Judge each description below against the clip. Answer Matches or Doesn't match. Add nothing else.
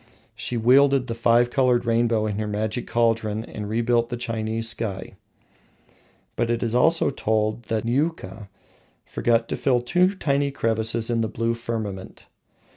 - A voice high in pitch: Doesn't match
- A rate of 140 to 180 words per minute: Matches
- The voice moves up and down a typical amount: Doesn't match